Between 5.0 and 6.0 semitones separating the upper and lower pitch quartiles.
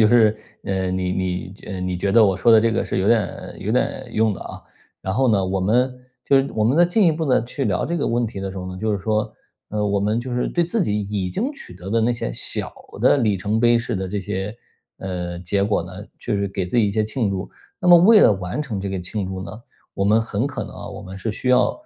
No: average, 4.0 semitones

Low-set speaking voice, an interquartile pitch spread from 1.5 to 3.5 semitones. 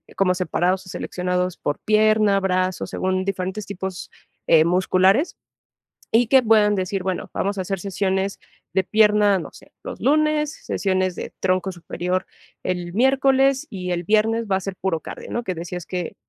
No: high, 190 Hz; average, 2.8 semitones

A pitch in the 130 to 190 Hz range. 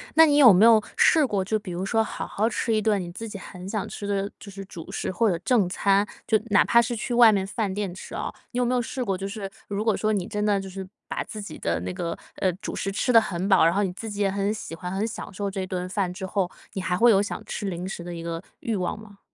No: high, 200 Hz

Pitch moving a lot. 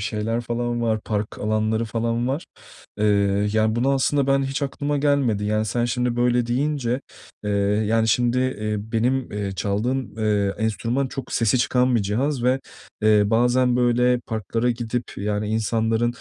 No: narrow, 2.6 semitones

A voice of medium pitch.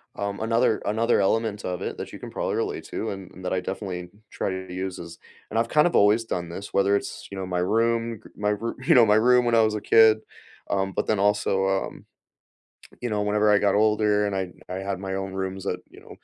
No: low, 100 Hz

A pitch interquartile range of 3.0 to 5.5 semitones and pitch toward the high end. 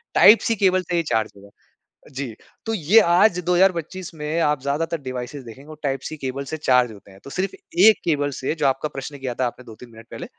No: average, 5.0 semitones; medium, 145 Hz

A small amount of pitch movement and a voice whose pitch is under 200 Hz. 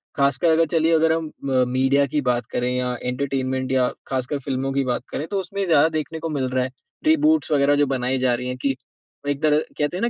No: average, 3.7 semitones; medium, 140 Hz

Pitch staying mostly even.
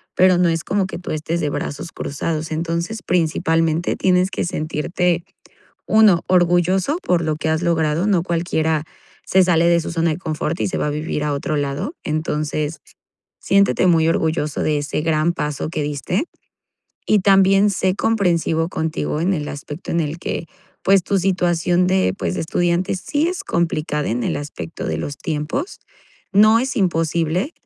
No: average, 3.1 semitones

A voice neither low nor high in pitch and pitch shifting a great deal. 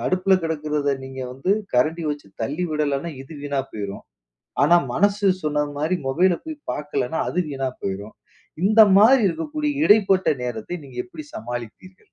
Yes: medium, 150 Hz; wide, 5.8 semitones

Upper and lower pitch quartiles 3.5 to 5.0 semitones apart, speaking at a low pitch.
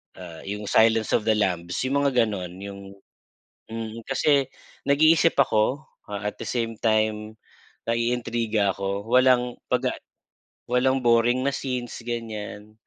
No: average, 3.1 semitones; low, 115 Hz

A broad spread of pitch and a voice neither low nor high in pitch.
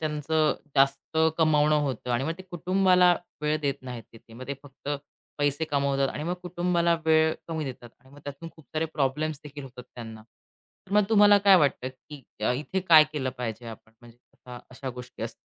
No: average, 3.6 semitones; medium, 145 Hz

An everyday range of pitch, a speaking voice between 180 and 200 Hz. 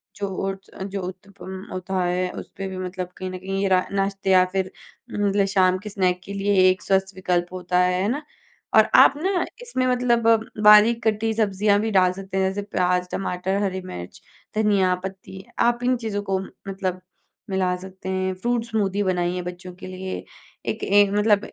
No: narrow, 1.9 semitones; high, 190 Hz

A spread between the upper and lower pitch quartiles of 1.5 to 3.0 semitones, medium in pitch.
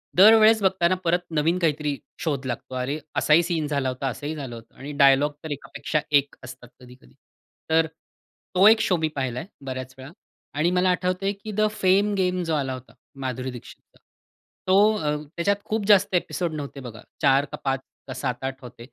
No: wide, 5.4 semitones; medium, 150 Hz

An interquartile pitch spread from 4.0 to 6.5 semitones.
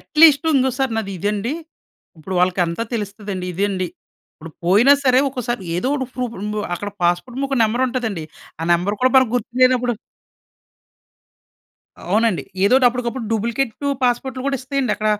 Yes: average, 4.4 semitones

